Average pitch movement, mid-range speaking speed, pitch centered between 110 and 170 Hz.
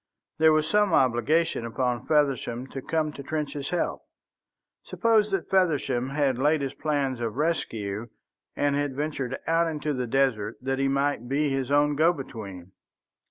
Yes: average, 3.4 semitones; average, 160 wpm; medium, 140 Hz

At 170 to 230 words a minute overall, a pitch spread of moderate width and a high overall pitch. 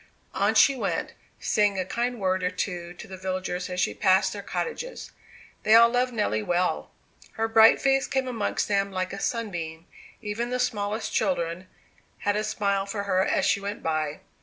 Yes: average, 185 wpm; average, 3.4 semitones; high, 200 Hz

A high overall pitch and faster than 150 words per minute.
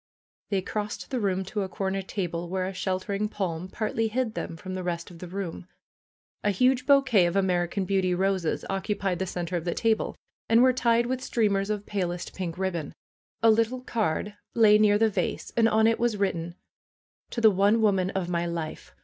Yes: high, 195 Hz; average, 200 wpm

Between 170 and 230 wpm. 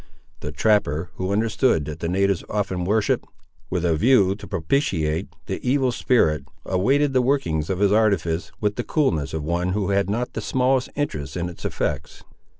Yes: average, 175 wpm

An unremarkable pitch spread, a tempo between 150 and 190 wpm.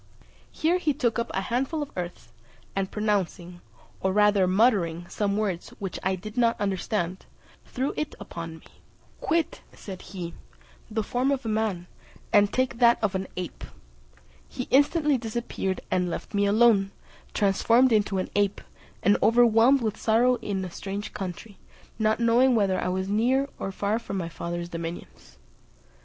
Yes: average, 4.0 semitones; average, 160 wpm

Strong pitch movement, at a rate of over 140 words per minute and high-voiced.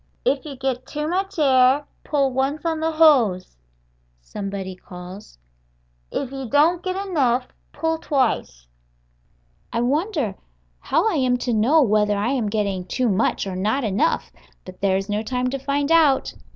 Yes: wide, 6.3 semitones; average, 160 wpm; very high, 255 Hz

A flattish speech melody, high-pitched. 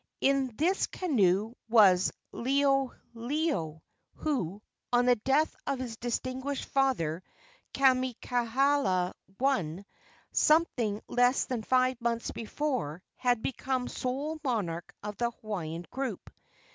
No: average, 4.5 semitones; high, 245 Hz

